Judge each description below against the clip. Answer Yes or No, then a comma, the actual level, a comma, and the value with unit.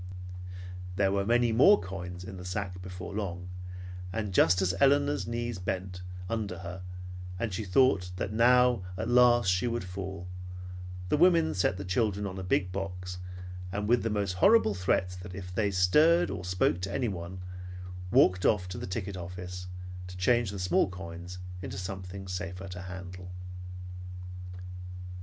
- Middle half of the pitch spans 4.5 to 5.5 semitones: No, average, 3.2 semitones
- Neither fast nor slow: Yes, average, 155 wpm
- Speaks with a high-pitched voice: No, very low, 95 Hz